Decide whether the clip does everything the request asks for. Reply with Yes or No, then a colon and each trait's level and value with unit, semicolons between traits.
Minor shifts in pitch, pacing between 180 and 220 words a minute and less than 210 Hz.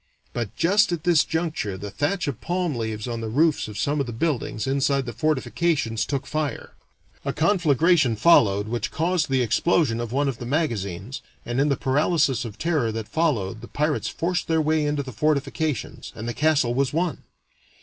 No: average, 5.3 semitones; average, 190 wpm; medium, 140 Hz